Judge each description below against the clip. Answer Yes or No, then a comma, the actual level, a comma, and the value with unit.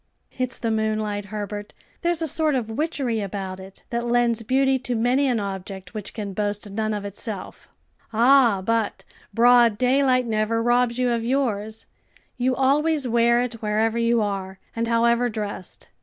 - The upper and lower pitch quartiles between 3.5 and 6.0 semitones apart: No, average, 3.0 semitones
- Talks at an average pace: Yes, average, 160 wpm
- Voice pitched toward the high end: Yes, high, 230 Hz